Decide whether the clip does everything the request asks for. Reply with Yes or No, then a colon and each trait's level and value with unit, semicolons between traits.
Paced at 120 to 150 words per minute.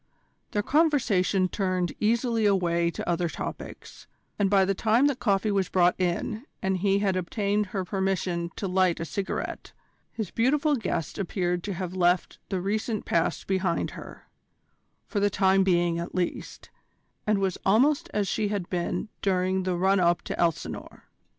No: average, 165 wpm